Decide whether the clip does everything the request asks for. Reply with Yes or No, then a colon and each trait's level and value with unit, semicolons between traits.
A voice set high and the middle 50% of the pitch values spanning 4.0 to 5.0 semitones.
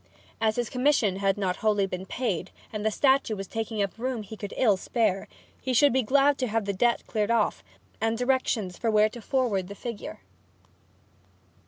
No: high, 220 Hz; average, 3.6 semitones